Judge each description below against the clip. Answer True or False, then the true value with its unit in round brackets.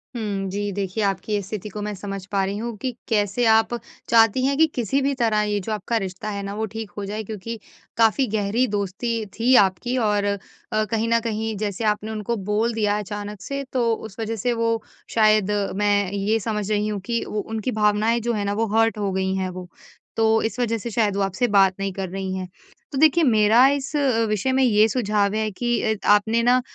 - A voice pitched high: True (215 Hz)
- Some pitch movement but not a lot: False (2.3 semitones)